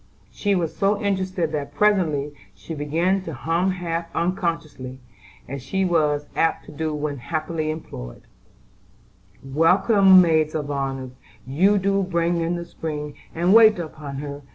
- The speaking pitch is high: No, medium, 165 Hz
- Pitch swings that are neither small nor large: Yes, average, 4.0 semitones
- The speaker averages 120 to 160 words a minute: Yes, average, 145 wpm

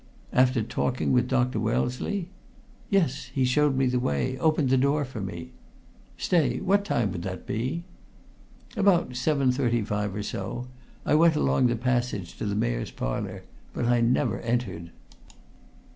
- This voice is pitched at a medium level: No, low, 125 Hz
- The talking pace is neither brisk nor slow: Yes, average, 150 wpm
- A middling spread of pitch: Yes, average, 3.9 semitones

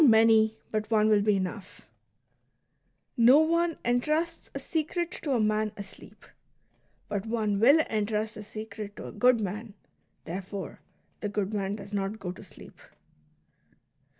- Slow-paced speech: No, average, 150 wpm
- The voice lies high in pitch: Yes, high, 215 Hz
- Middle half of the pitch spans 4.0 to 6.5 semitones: No, average, 2.9 semitones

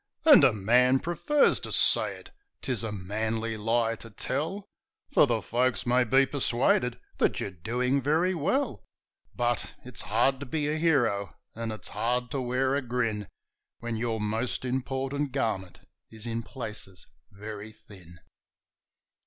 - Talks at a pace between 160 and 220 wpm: No, average, 150 wpm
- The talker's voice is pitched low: Yes, low, 120 Hz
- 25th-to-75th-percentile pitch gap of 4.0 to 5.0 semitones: No, average, 3.5 semitones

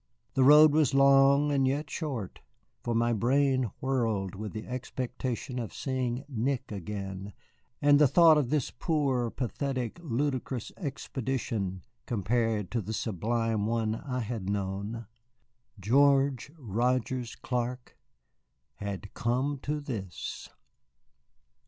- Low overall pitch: Yes, low, 125 Hz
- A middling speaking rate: No, slow, 115 wpm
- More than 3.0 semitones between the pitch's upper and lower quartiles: Yes, average, 3.9 semitones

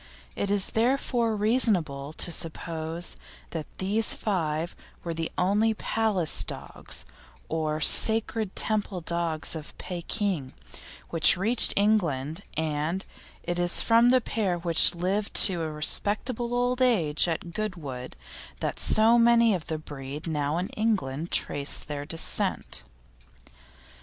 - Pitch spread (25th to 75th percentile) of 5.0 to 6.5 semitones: Yes, wide, 5.5 semitones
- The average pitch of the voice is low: No, medium, 175 Hz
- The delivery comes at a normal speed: No, slow, 125 wpm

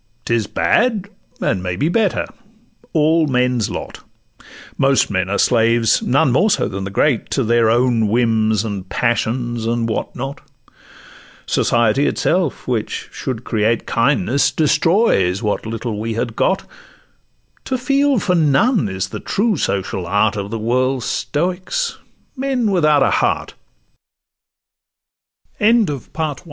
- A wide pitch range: Yes, wide, 6.0 semitones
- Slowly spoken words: Yes, slow, 120 wpm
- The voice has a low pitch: Yes, low, 120 Hz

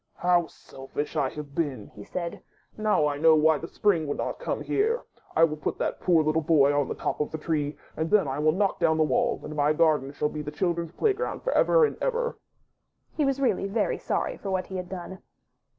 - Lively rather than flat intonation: No, average, 4.3 semitones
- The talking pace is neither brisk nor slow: No, fast, 230 wpm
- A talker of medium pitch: Yes, medium, 160 Hz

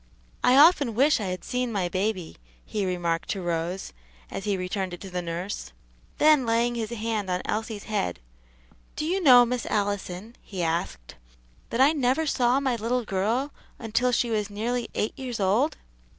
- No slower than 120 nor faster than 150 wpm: No, average, 175 wpm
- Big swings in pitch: No, average, 4.9 semitones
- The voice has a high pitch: Yes, high, 220 Hz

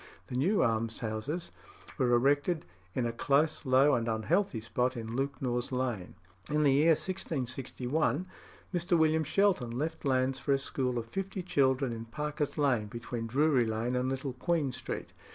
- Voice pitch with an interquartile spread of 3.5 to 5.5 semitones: Yes, average, 4.1 semitones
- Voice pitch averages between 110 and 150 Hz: Yes, low, 135 Hz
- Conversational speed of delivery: Yes, average, 155 wpm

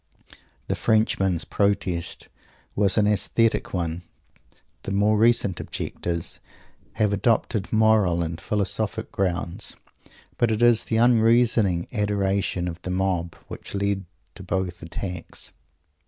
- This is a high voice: No, low, 100 Hz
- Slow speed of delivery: Yes, slow, 115 wpm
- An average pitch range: Yes, average, 3.4 semitones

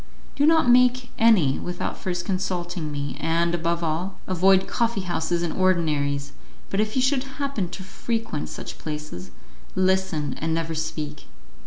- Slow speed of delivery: No, average, 150 wpm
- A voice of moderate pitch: Yes, medium, 175 Hz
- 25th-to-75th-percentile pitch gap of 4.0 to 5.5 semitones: Yes, average, 4.9 semitones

